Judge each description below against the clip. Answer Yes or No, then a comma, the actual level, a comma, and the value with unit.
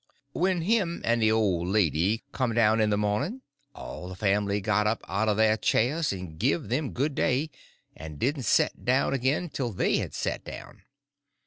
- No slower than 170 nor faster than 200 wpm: Yes, average, 185 wpm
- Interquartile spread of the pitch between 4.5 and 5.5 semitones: Yes, average, 5.2 semitones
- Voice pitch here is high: No, low, 110 Hz